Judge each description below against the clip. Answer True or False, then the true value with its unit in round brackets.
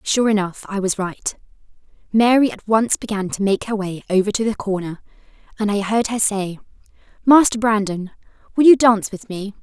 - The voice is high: True (210 Hz)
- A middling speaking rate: True (180 wpm)